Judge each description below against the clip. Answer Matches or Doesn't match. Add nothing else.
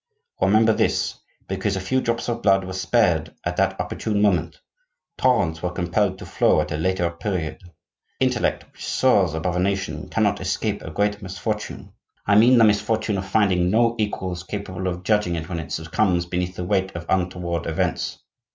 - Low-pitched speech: Matches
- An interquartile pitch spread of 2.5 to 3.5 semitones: Matches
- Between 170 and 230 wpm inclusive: Matches